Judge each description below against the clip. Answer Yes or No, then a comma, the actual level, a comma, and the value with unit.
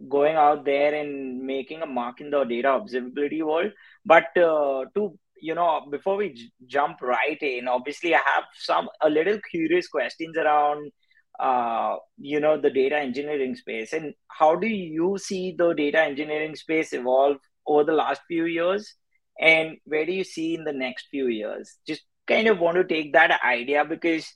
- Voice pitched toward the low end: No, medium, 155 Hz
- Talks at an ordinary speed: Yes, average, 180 wpm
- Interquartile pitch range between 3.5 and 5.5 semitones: No, average, 2.8 semitones